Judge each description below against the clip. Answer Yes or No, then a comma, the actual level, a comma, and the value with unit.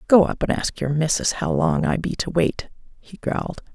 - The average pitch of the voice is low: No, medium, 170 Hz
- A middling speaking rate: No, fast, 225 wpm